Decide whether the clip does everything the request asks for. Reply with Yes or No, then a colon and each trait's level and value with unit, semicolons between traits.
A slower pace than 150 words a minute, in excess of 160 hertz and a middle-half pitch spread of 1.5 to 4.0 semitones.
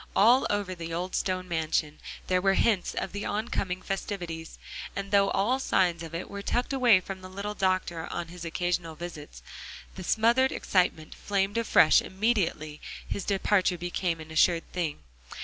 No: average, 165 wpm; medium, 185 Hz; average, 3.1 semitones